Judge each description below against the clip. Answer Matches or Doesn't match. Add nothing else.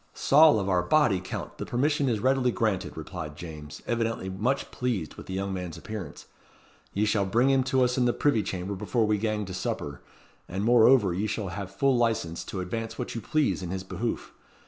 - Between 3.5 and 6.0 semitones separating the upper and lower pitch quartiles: Matches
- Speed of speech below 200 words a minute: Doesn't match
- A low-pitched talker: Matches